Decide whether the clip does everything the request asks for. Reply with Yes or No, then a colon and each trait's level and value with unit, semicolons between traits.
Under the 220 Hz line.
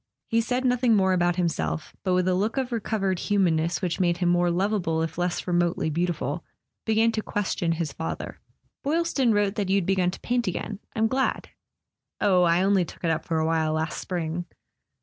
Yes: medium, 185 Hz